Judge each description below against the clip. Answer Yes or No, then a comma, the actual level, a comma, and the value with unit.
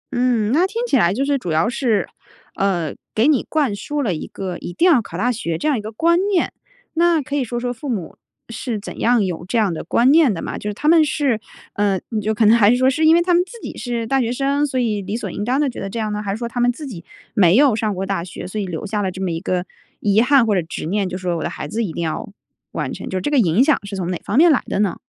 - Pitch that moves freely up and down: Yes, wide, 5.8 semitones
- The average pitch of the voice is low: No, high, 225 Hz